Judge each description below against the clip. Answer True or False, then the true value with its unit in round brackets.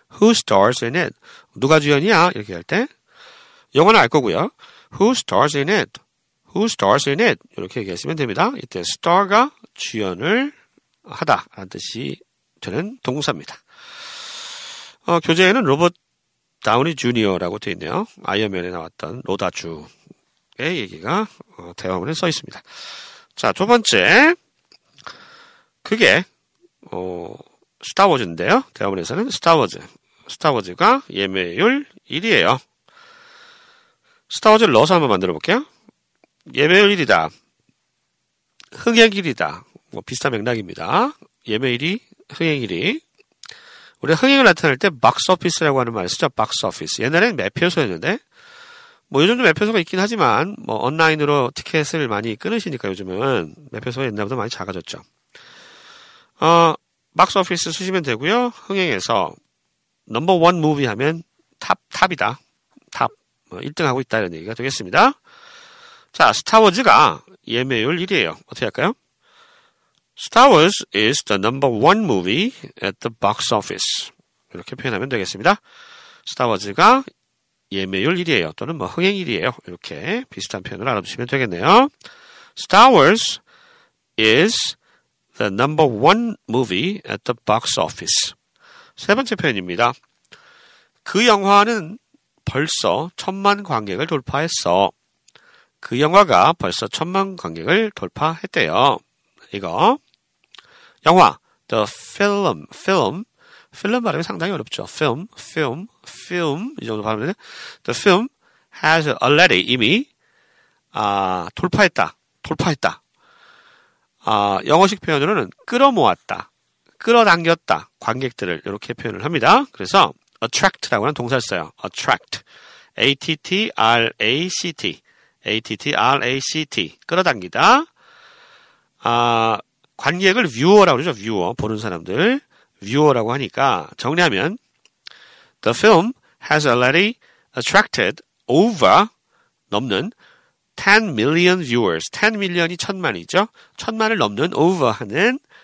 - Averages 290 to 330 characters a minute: True (325 characters per minute)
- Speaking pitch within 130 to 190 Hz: True (185 Hz)